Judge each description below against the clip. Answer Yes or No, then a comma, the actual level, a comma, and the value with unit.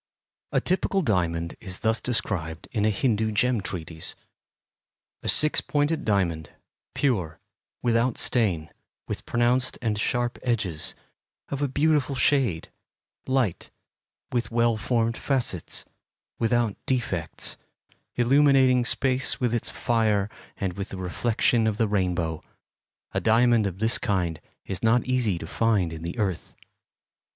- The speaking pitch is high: No, low, 115 Hz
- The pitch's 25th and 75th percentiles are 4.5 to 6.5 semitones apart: Yes, average, 4.9 semitones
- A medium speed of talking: No, slow, 130 wpm